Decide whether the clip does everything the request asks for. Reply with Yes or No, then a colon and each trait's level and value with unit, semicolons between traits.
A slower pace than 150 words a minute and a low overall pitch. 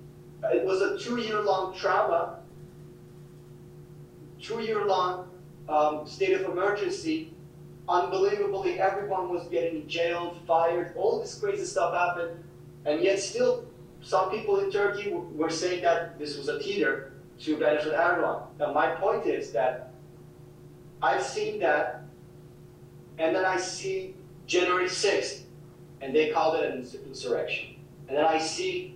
No: slow, 135 wpm; medium, 180 Hz